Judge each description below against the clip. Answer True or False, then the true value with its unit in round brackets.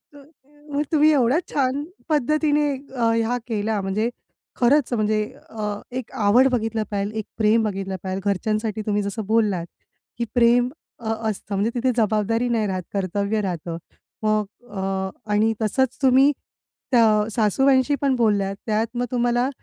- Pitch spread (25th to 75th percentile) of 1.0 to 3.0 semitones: False (3.7 semitones)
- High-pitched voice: True (225 Hz)